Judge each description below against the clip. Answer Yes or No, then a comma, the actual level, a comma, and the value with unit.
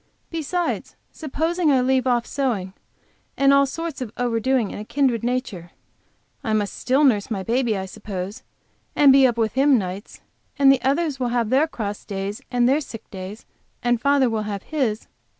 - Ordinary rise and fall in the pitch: Yes, average, 4.5 semitones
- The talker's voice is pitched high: Yes, high, 245 Hz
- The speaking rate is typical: Yes, average, 170 wpm